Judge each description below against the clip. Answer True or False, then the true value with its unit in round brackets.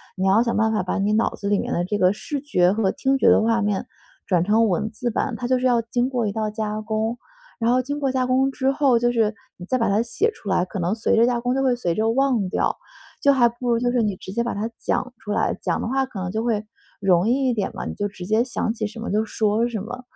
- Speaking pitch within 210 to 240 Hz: True (225 Hz)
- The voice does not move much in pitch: False (3.1 semitones)